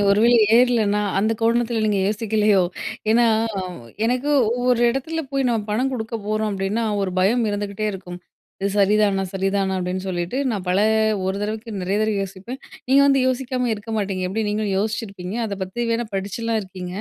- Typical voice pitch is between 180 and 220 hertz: Yes, high, 215 Hz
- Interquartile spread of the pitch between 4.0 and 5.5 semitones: No, average, 3.4 semitones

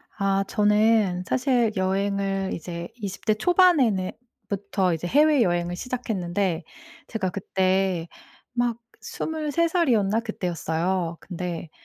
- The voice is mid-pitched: No, high, 195 Hz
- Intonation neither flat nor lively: Yes, average, 4.5 semitones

